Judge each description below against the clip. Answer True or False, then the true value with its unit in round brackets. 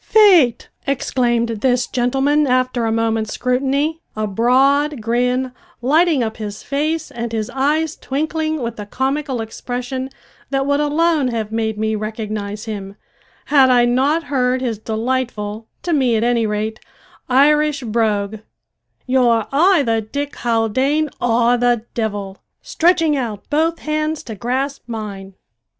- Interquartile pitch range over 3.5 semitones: True (4.2 semitones)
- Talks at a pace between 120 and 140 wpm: True (135 wpm)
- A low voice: False (250 Hz)